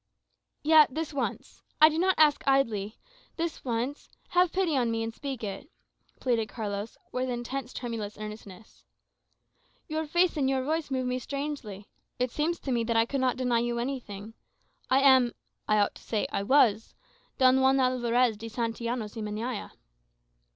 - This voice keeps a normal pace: Yes, average, 165 wpm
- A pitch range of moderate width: Yes, average, 3.6 semitones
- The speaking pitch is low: No, very high, 250 Hz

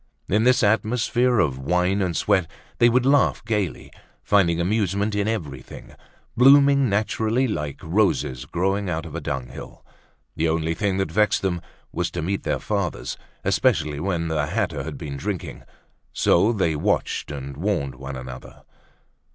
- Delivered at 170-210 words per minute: No, average, 150 wpm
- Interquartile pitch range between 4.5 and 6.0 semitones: Yes, wide, 5.5 semitones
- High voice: No, very low, 95 Hz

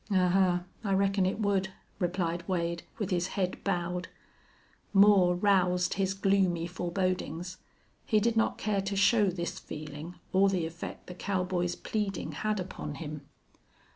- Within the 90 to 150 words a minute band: Yes, average, 140 wpm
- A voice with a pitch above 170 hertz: Yes, medium, 185 Hz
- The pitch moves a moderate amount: No, narrow, 2.0 semitones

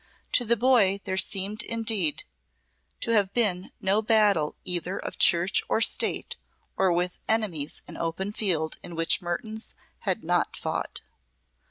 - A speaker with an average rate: Yes, average, 145 wpm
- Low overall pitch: No, high, 195 Hz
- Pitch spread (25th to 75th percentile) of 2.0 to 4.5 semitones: Yes, average, 3.9 semitones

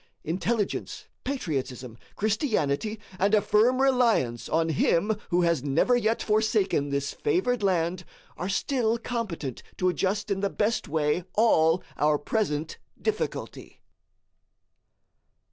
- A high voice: Yes, high, 195 Hz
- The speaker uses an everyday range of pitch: No, wide, 6.0 semitones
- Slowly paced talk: Yes, slow, 115 wpm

